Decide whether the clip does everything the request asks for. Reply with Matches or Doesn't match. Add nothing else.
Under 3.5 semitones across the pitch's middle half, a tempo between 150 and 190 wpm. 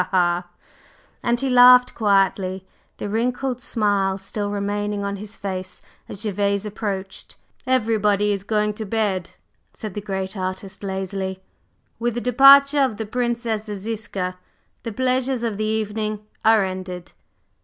Doesn't match